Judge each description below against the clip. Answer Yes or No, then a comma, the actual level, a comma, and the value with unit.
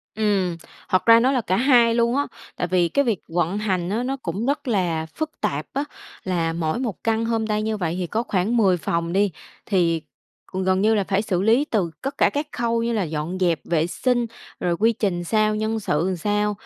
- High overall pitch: Yes, high, 205 Hz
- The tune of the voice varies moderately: Yes, average, 4.7 semitones